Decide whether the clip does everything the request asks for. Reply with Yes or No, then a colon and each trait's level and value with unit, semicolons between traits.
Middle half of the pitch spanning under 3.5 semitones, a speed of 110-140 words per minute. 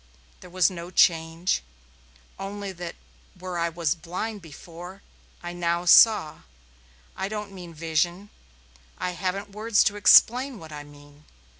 Yes: average, 3.1 semitones; slow, 135 wpm